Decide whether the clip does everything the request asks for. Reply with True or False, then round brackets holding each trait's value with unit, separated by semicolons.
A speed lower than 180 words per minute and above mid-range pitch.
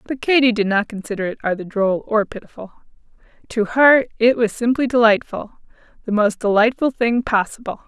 True (150 wpm; 225 Hz)